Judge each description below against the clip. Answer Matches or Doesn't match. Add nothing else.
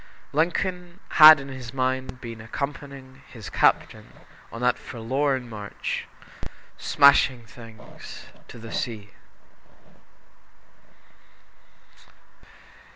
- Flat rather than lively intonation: Doesn't match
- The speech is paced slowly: Matches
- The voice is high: Doesn't match